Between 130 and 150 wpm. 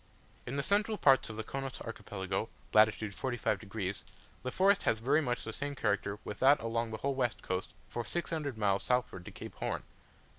No: average, 190 wpm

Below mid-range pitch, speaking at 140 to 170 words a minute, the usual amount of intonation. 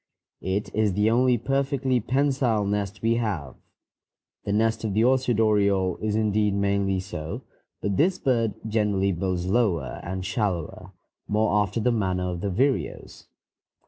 Yes: low, 105 Hz; average, 145 wpm; average, 3.3 semitones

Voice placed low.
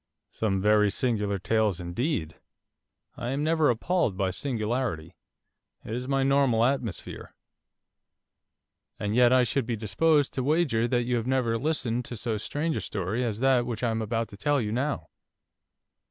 Yes: low, 120 Hz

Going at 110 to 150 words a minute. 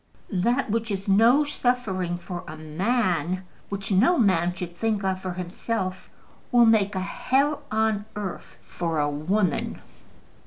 Yes: average, 145 wpm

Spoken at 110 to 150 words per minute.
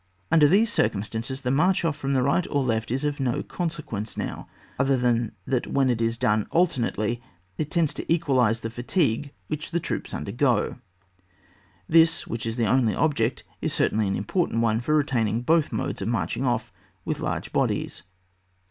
No: average, 180 wpm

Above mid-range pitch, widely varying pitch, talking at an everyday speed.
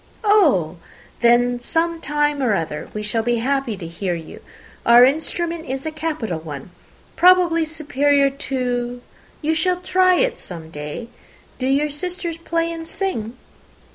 Yes: very high, 275 Hz; wide, 6.3 semitones; average, 145 wpm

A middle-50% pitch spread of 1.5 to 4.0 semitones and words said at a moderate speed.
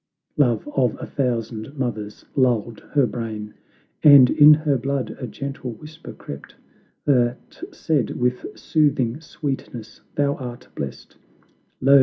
No: average, 3.6 semitones; slow, 125 wpm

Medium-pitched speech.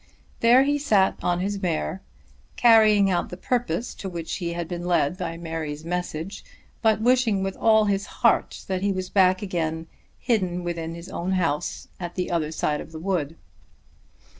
Yes: medium, 180 Hz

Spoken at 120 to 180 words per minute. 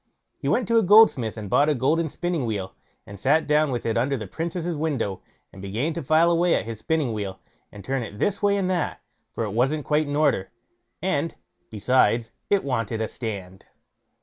No: fast, 205 wpm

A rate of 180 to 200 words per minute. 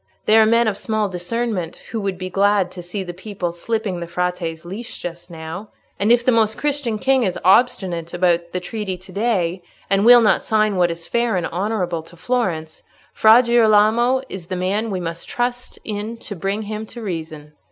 Yes: average, 195 wpm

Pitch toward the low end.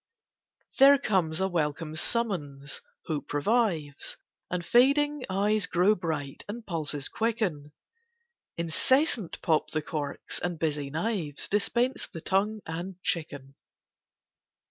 No: medium, 175 Hz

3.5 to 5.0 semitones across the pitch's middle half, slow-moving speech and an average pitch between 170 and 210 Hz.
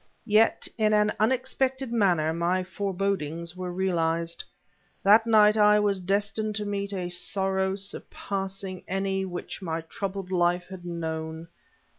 No: average, 2.9 semitones; slow, 130 wpm; high, 190 Hz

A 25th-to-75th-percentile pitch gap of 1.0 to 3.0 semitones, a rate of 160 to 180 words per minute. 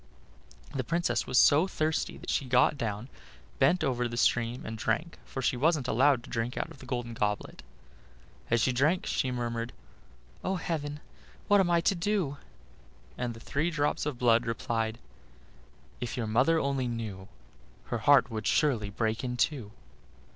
No: average, 4.2 semitones; average, 170 wpm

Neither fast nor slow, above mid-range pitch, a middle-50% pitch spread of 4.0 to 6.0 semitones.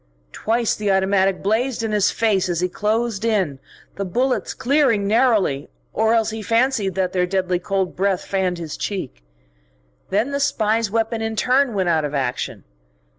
No: average, 170 wpm; high, 205 Hz; average, 3.5 semitones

